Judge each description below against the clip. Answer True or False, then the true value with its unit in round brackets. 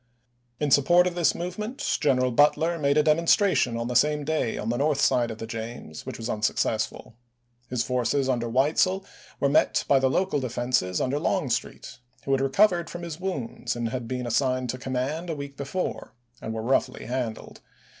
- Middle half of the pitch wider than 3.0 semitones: True (4.5 semitones)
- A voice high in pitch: False (135 Hz)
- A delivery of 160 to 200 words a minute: True (180 wpm)